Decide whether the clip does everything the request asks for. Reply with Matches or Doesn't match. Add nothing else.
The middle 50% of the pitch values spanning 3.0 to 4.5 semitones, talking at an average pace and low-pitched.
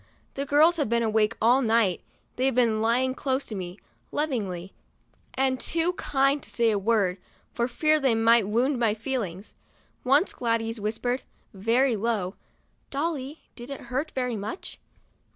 Doesn't match